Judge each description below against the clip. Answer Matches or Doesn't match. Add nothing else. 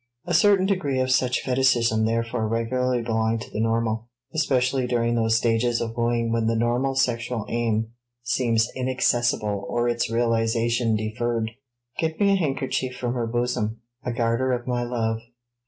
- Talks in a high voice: Doesn't match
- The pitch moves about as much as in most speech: Doesn't match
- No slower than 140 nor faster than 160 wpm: Matches